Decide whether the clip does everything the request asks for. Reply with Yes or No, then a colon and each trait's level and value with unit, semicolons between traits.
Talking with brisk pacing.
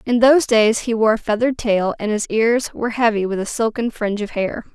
Yes: fast, 240 wpm